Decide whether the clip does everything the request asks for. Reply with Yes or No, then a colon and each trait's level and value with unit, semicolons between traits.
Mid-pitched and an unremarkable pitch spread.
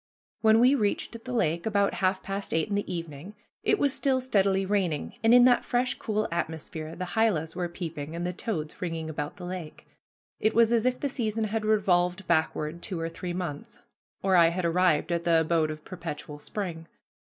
Yes: medium, 180 Hz; average, 4.8 semitones